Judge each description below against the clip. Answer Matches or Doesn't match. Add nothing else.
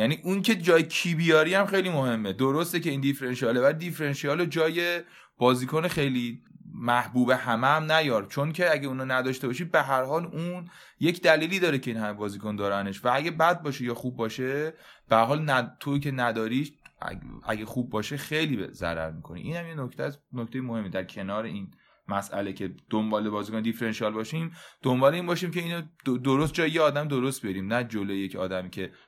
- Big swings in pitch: Matches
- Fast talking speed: Matches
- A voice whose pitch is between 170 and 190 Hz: Doesn't match